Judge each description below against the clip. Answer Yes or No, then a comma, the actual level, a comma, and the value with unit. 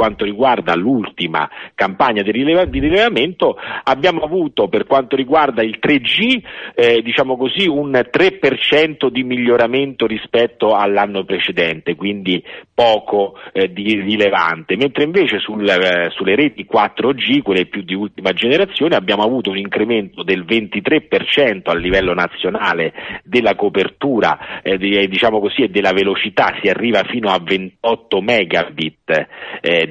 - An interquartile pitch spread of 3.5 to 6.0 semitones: Yes, average, 5.0 semitones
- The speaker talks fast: No, average, 130 wpm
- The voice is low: Yes, low, 105 Hz